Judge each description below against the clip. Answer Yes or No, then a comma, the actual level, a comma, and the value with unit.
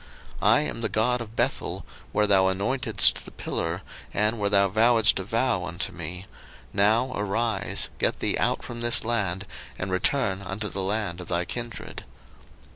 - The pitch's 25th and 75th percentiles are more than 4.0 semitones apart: No, average, 3.5 semitones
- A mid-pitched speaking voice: No, low, 105 Hz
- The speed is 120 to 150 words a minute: No, average, 170 wpm